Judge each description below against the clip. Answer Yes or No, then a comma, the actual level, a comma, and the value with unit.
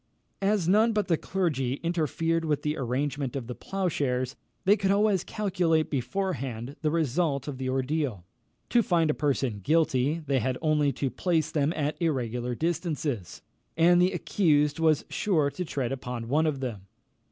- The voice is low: No, medium, 150 Hz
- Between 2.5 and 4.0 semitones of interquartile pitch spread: No, average, 4.6 semitones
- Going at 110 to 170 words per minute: Yes, average, 165 wpm